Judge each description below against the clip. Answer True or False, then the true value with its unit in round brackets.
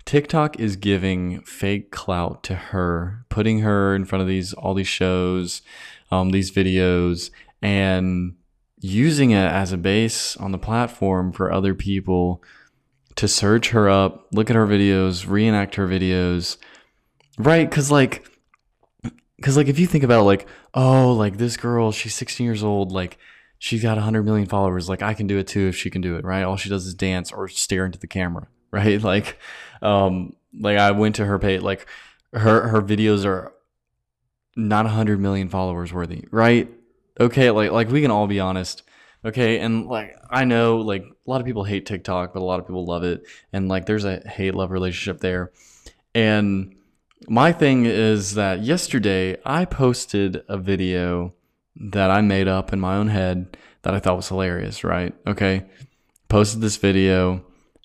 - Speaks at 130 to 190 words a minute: True (180 wpm)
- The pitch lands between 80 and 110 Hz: True (100 Hz)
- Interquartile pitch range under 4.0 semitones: True (3.0 semitones)